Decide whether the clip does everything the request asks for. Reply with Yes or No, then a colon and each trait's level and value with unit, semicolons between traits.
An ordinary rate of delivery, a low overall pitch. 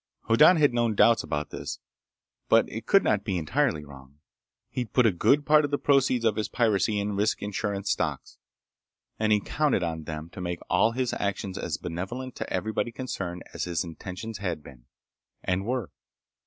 Yes: average, 180 wpm; low, 105 Hz